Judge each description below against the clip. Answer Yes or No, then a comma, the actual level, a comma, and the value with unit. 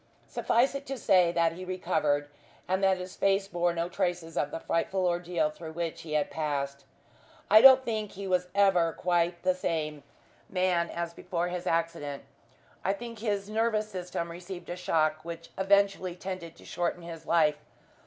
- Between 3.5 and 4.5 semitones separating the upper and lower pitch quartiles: No, narrow, 2.5 semitones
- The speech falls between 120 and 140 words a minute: No, average, 175 wpm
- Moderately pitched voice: Yes, medium, 175 Hz